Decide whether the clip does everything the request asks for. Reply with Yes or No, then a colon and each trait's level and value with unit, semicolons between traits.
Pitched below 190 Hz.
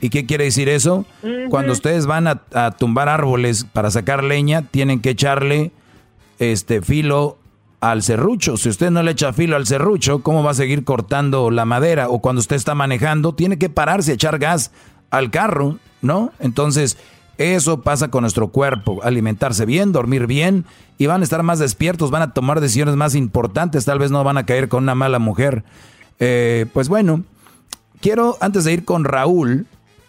Yes: medium, 140 Hz